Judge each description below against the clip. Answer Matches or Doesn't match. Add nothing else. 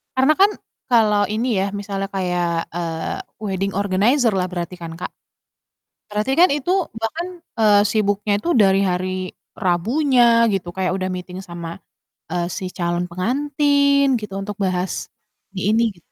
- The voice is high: Matches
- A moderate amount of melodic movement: Matches